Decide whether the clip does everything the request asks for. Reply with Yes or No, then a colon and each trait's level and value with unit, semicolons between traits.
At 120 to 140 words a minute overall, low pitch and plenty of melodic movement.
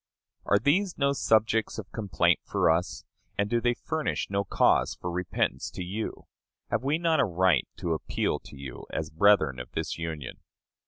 No: average, 175 wpm; low, 100 Hz; wide, 6.5 semitones